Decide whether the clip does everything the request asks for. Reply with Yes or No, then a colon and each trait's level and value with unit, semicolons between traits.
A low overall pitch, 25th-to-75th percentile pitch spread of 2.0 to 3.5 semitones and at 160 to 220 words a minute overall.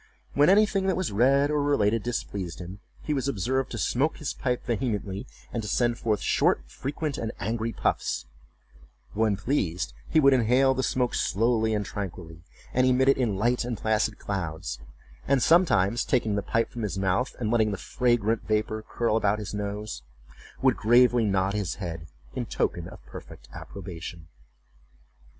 No: low, 110 Hz; average, 4.2 semitones; average, 170 wpm